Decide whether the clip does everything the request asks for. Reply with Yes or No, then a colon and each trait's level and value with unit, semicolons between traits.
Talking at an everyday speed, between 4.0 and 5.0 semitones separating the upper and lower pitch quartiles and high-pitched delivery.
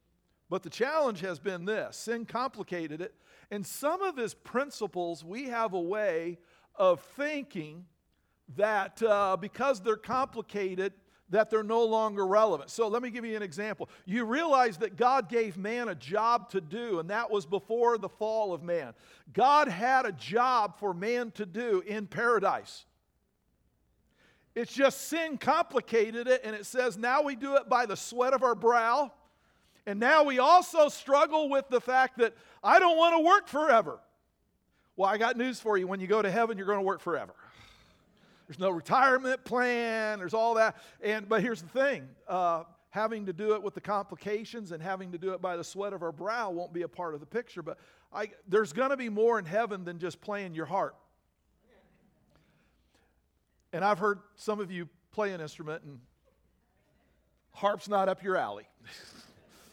Yes: average, 180 wpm; average, 4.3 semitones; high, 215 Hz